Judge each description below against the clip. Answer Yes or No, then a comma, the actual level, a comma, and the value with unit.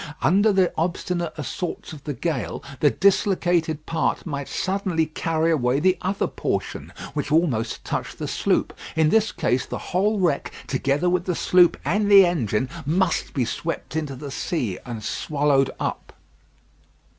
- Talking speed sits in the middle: Yes, average, 155 wpm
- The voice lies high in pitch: No, medium, 160 Hz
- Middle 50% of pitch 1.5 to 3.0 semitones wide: No, average, 4.3 semitones